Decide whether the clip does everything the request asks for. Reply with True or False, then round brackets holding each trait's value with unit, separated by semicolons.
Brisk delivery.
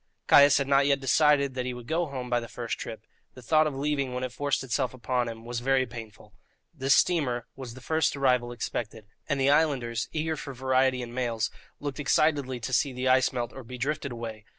True (220 wpm)